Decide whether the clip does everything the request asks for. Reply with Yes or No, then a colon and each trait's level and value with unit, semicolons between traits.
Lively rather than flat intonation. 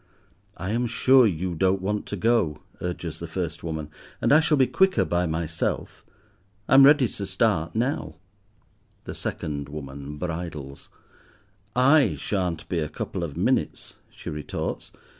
Yes: wide, 6.8 semitones